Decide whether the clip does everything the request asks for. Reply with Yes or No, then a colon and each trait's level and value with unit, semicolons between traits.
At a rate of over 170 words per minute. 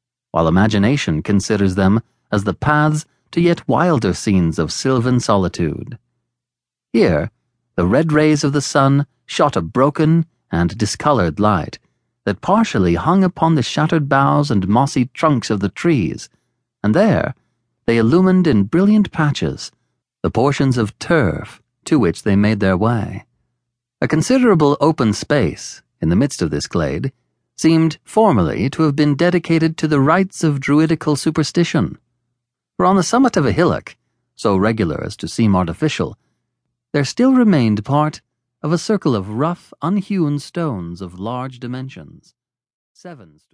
No: average, 150 wpm